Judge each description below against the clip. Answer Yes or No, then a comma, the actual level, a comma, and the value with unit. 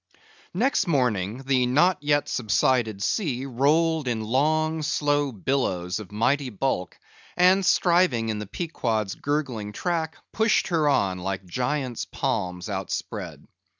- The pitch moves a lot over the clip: Yes, wide, 6.5 semitones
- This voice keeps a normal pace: No, slow, 125 wpm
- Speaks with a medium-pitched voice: No, low, 130 Hz